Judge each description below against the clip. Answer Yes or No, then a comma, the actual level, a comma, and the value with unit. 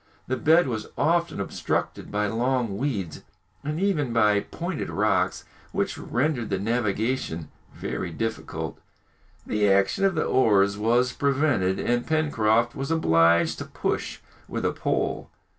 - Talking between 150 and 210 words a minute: No, slow, 135 wpm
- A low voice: Yes, low, 120 Hz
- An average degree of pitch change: No, wide, 6.1 semitones